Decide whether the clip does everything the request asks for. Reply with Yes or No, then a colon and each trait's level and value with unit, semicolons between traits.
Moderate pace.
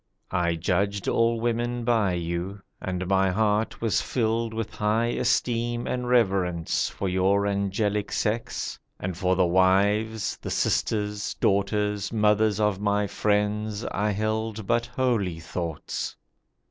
No: slow, 130 wpm